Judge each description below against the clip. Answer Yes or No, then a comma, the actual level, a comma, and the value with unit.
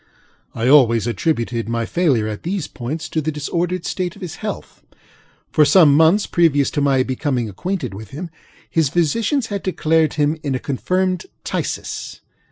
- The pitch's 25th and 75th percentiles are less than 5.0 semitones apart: No, average, 5.3 semitones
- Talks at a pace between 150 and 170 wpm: Yes, average, 165 wpm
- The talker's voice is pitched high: No, medium, 150 Hz